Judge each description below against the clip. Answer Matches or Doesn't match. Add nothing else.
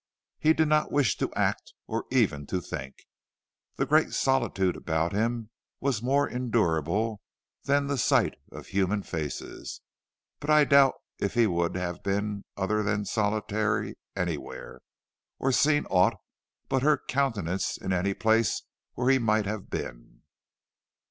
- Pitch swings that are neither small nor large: Doesn't match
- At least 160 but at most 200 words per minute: Doesn't match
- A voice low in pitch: Matches